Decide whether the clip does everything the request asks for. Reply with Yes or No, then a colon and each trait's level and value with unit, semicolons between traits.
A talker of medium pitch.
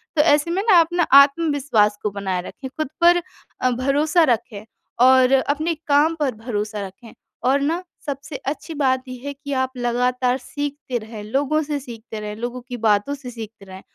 No: very high, 260 Hz